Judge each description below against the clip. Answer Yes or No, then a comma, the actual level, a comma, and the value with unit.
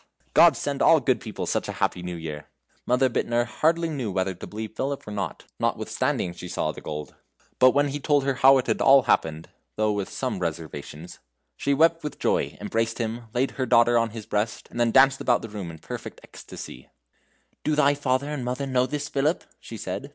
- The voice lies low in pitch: Yes, low, 120 Hz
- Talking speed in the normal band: No, fast, 215 wpm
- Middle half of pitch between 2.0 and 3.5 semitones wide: No, wide, 5.4 semitones